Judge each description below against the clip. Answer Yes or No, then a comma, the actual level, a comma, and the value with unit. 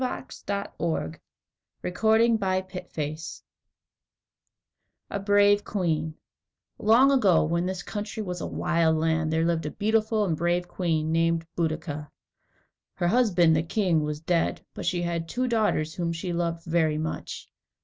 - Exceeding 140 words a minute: No, slow, 135 wpm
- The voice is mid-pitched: Yes, medium, 170 Hz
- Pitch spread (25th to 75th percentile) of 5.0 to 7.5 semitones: No, average, 4.0 semitones